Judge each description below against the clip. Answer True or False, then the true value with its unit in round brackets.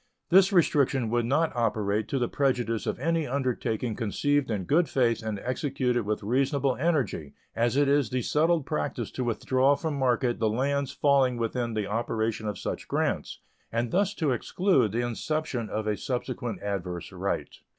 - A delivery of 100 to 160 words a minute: False (170 wpm)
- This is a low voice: True (125 Hz)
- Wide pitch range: False (4.1 semitones)